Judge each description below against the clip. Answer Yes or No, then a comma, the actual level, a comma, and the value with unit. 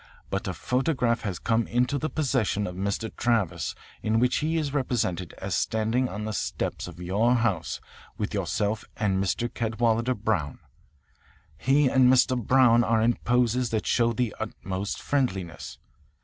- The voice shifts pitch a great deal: No, average, 3.7 semitones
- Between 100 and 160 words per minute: Yes, average, 155 wpm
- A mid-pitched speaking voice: No, low, 115 Hz